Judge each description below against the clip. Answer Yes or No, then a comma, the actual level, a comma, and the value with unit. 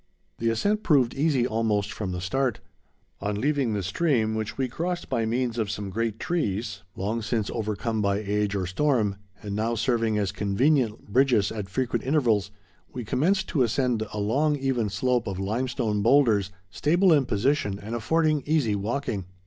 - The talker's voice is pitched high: No, low, 115 Hz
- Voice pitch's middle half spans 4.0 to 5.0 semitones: Yes, average, 4.7 semitones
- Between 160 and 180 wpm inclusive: Yes, average, 170 wpm